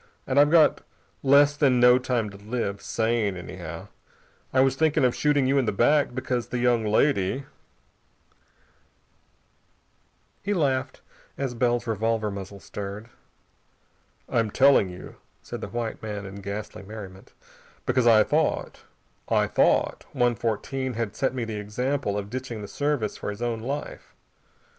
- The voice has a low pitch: Yes, low, 120 Hz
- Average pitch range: Yes, average, 4.1 semitones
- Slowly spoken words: No, average, 150 wpm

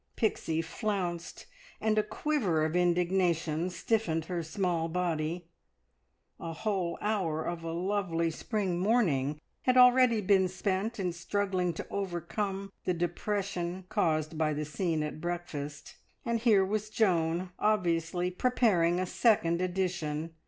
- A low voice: No, medium, 180 Hz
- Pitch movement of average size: Yes, average, 3.6 semitones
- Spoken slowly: Yes, slow, 130 wpm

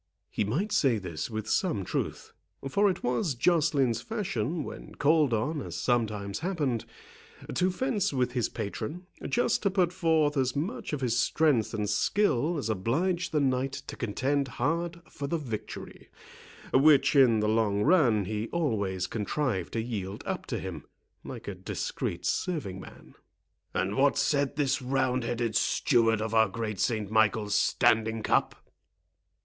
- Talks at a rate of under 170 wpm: Yes, average, 155 wpm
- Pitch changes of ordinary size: No, wide, 6.2 semitones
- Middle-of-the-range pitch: No, low, 125 Hz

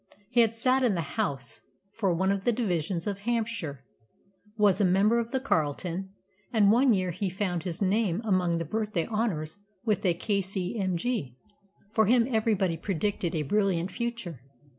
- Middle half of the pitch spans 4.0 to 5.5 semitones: Yes, average, 4.4 semitones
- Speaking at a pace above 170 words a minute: No, average, 160 wpm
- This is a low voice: No, high, 195 Hz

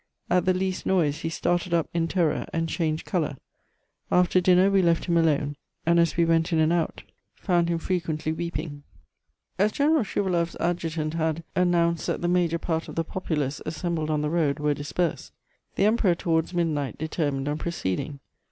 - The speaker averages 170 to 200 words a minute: Yes, average, 180 wpm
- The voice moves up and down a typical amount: No, narrow, 2.1 semitones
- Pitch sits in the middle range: Yes, medium, 165 Hz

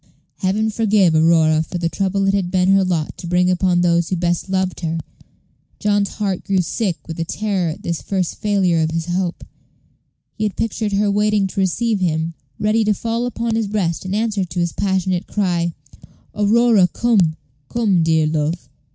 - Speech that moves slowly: No, average, 180 wpm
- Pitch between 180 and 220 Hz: Yes, medium, 185 Hz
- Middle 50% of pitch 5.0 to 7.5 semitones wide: No, average, 3.4 semitones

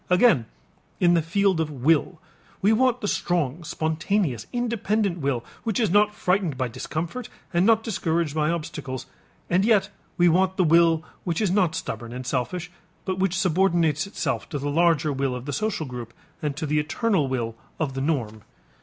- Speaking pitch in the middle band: Yes, medium, 165 Hz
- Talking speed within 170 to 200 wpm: Yes, average, 180 wpm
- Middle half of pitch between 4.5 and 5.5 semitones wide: Yes, average, 5.1 semitones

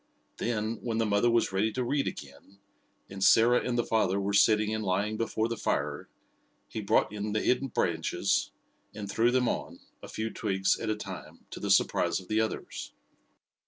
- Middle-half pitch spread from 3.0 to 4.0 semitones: No, narrow, 2.6 semitones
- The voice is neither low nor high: No, low, 110 Hz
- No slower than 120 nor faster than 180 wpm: No, average, 190 wpm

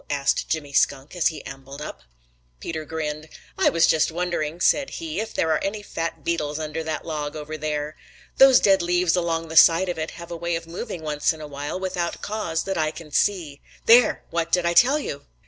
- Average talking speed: No, fast, 215 wpm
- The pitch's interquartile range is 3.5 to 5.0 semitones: No, average, 2.7 semitones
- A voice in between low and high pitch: Yes, medium, 165 Hz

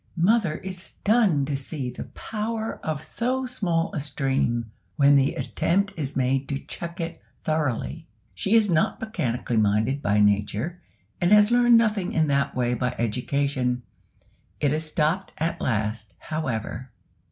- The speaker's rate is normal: Yes, average, 150 wpm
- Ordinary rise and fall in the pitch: No, wide, 7.0 semitones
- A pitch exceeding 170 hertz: No, medium, 150 Hz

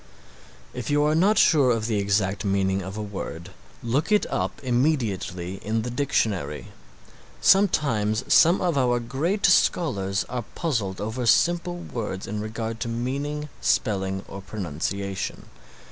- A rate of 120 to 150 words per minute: Yes, average, 140 wpm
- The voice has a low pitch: Yes, low, 115 Hz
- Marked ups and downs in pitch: Yes, wide, 6.6 semitones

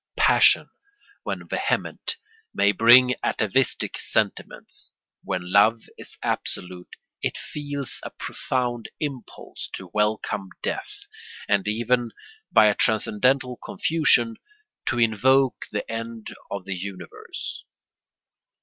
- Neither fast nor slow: No, slow, 105 wpm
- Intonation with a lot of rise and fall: No, average, 4.0 semitones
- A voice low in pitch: Yes, low, 115 Hz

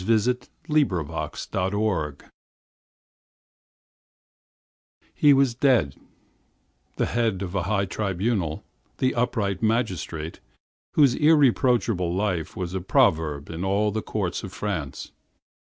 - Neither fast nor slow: No, slow, 105 wpm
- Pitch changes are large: No, average, 5.0 semitones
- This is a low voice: Yes, low, 100 Hz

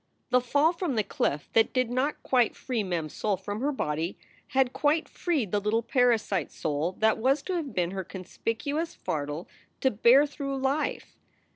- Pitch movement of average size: No, wide, 6.4 semitones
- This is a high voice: Yes, high, 235 Hz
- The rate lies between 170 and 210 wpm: Yes, average, 180 wpm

